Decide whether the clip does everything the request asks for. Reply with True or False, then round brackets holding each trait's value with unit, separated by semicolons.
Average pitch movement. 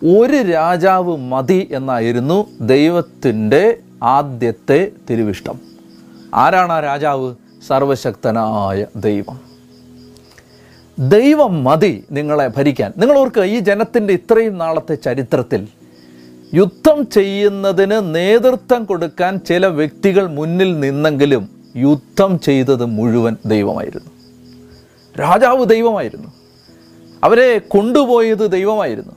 False (9.0 semitones)